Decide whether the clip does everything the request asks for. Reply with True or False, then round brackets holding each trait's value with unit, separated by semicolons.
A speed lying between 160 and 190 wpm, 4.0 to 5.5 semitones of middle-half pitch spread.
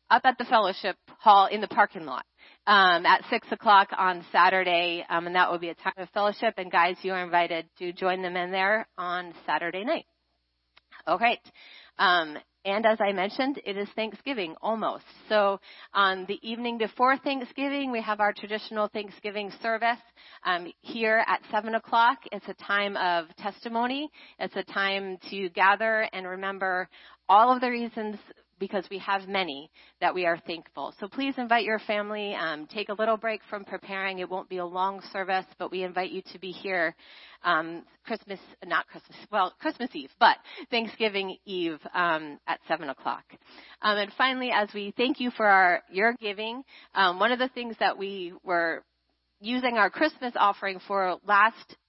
False (175 wpm; 3.6 semitones)